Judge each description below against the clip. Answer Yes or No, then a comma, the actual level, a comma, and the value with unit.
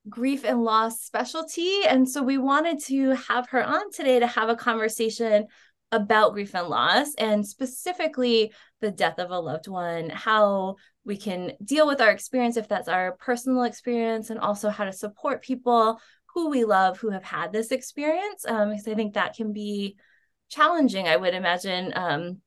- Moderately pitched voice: No, high, 225 Hz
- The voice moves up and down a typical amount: Yes, average, 4.1 semitones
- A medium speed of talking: Yes, average, 180 wpm